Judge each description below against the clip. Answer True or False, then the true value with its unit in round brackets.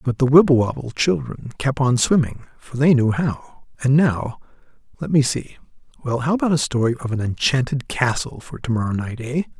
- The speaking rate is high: False (190 wpm)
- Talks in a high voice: False (130 Hz)